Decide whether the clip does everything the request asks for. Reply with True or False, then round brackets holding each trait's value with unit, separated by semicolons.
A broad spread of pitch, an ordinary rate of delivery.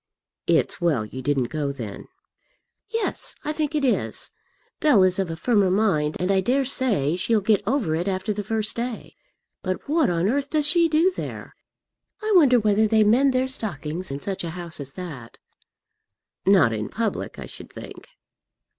True (7.8 semitones; 180 wpm)